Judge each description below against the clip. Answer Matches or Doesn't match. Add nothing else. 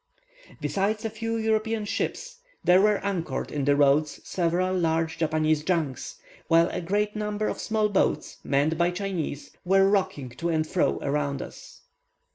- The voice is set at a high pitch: Doesn't match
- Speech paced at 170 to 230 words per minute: Doesn't match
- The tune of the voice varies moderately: Matches